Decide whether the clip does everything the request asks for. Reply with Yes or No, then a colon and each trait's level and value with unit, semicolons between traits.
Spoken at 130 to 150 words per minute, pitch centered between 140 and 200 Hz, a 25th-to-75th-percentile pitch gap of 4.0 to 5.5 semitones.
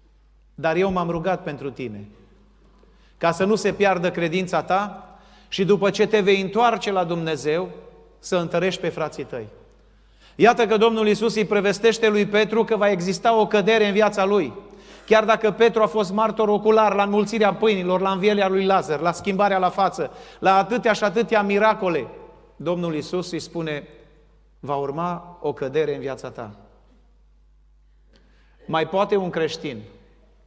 No: average, 160 wpm; high, 190 Hz; average, 4.6 semitones